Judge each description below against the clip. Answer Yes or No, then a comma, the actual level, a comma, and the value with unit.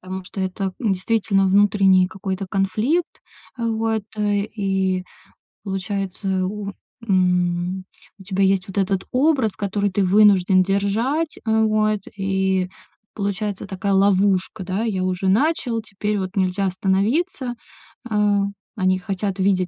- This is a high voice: Yes, high, 195 Hz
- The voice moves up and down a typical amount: No, narrow, 2.0 semitones